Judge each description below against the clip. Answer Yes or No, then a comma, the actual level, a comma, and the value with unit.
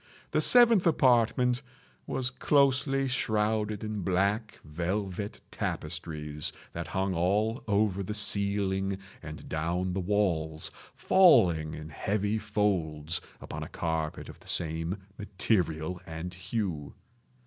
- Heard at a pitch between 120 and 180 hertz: No, very low, 95 Hz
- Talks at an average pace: No, slow, 115 wpm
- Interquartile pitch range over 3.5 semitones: Yes, average, 4.6 semitones